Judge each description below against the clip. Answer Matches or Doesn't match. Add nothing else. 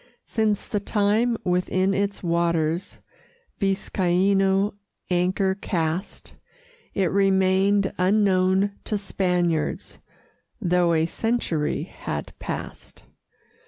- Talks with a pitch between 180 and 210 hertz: Matches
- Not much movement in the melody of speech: Matches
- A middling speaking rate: Doesn't match